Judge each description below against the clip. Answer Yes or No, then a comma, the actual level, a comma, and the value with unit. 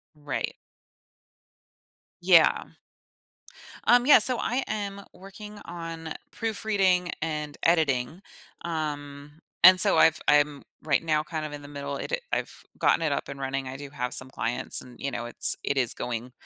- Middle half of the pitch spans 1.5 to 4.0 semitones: No, average, 4.6 semitones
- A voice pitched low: No, medium, 150 Hz